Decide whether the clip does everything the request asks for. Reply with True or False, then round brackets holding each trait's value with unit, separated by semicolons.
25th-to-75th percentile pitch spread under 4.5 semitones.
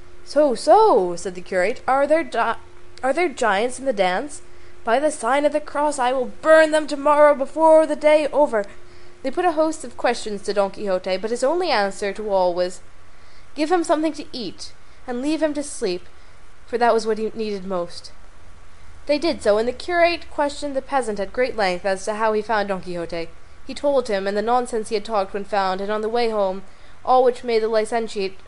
False (6.7 semitones)